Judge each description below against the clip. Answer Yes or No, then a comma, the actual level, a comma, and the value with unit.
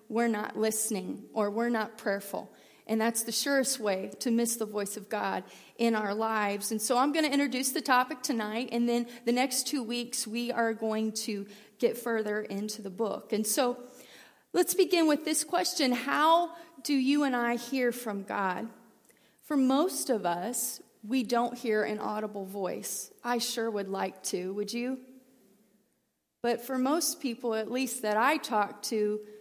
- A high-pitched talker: Yes, high, 235 Hz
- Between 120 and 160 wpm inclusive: No, average, 180 wpm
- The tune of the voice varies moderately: Yes, average, 3.3 semitones